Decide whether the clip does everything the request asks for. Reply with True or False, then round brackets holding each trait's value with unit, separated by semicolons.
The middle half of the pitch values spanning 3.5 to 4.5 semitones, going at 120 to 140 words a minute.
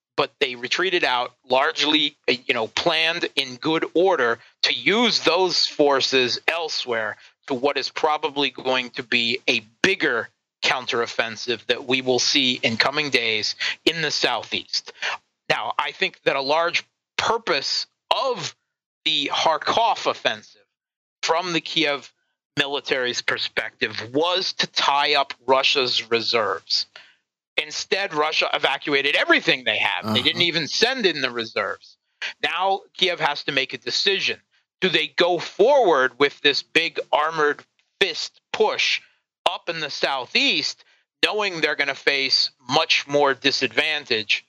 True (3.9 semitones; 135 wpm)